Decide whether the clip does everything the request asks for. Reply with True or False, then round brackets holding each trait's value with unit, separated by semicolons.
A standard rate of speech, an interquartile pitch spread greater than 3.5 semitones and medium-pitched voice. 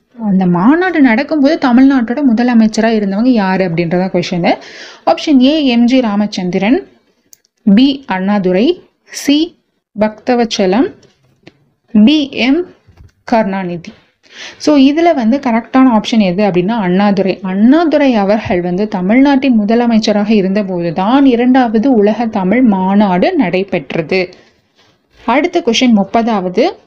False (95 wpm; 5.3 semitones; 225 Hz)